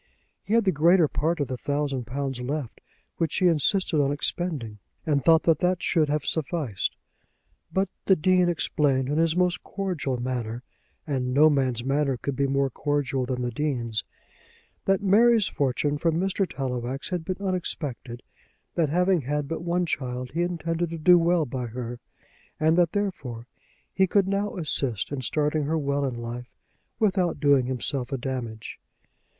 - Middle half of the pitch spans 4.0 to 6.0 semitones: Yes, average, 5.1 semitones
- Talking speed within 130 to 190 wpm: Yes, average, 165 wpm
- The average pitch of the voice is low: No, medium, 145 Hz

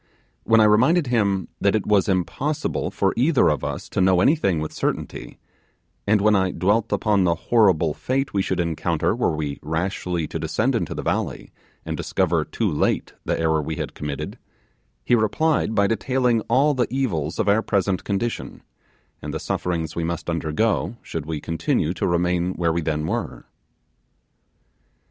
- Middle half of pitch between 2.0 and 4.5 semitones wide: No, wide, 5.4 semitones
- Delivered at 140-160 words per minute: No, average, 170 wpm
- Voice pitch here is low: Yes, very low, 95 Hz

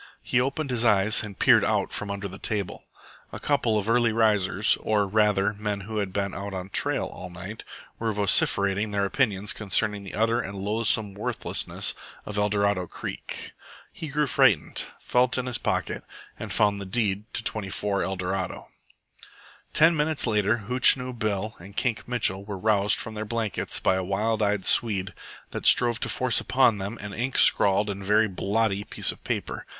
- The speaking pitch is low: Yes, low, 105 Hz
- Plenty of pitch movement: No, narrow, 2.5 semitones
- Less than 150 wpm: No, average, 175 wpm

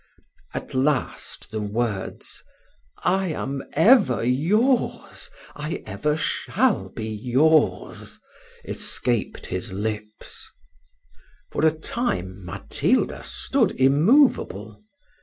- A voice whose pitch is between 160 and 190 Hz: No, low, 130 Hz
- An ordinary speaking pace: No, slow, 85 wpm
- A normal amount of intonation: No, wide, 6.9 semitones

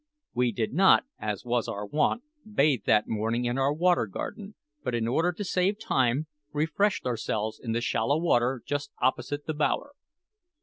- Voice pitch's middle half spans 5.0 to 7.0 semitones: Yes, wide, 5.6 semitones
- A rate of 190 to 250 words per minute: No, average, 170 wpm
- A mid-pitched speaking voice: No, low, 130 Hz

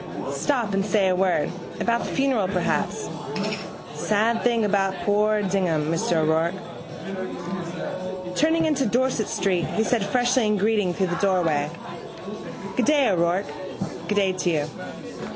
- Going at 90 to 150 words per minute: Yes, average, 140 wpm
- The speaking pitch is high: Yes, high, 195 Hz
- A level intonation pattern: No, average, 3.6 semitones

